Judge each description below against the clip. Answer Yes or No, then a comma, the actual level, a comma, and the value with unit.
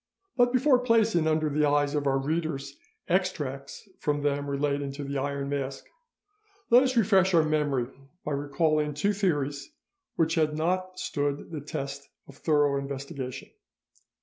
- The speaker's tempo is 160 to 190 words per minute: No, average, 150 wpm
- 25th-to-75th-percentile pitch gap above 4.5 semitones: No, average, 3.4 semitones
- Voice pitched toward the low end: No, medium, 145 Hz